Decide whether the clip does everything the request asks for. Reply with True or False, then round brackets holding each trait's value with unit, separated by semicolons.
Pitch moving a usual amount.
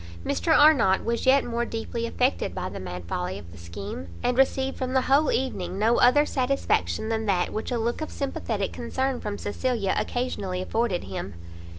False (6.1 semitones)